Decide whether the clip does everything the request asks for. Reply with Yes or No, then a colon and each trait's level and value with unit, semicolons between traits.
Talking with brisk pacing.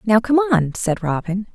No: average, 195 wpm